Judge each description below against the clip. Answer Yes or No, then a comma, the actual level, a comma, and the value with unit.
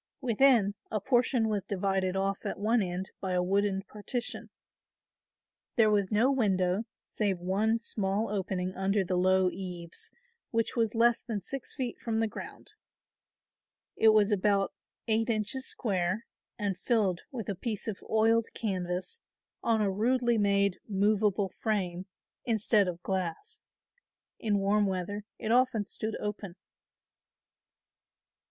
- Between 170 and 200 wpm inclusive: No, slow, 135 wpm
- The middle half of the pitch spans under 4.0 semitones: Yes, average, 2.9 semitones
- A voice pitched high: Yes, high, 205 Hz